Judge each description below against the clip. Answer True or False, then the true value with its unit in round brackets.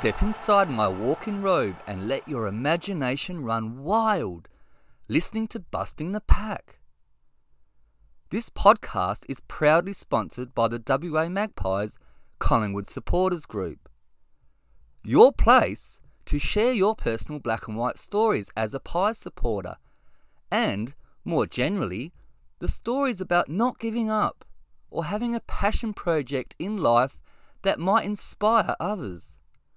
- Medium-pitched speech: True (155 Hz)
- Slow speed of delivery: True (125 wpm)